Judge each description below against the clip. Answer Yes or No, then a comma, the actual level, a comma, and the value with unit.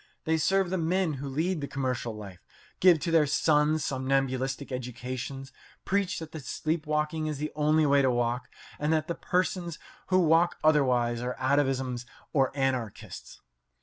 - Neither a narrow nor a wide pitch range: Yes, average, 3.7 semitones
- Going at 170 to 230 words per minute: No, average, 155 wpm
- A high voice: No, medium, 145 Hz